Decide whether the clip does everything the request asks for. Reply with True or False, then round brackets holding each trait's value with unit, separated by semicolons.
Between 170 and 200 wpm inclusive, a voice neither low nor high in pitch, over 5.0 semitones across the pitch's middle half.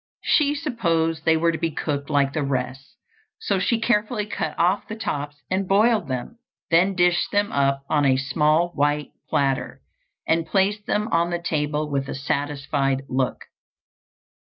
False (160 wpm; 160 Hz; 5.5 semitones)